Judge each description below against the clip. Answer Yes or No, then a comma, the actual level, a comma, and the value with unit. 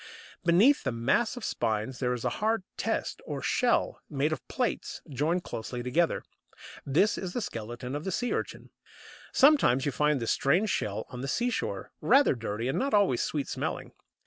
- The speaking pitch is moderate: Yes, medium, 150 Hz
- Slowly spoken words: No, average, 175 wpm